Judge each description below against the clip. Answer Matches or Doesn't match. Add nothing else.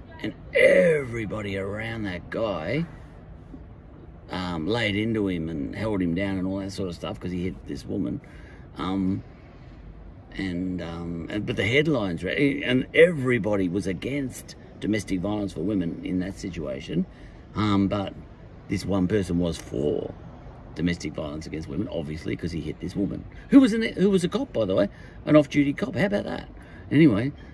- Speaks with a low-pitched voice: Matches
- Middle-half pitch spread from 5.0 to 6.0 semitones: Matches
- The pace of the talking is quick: Doesn't match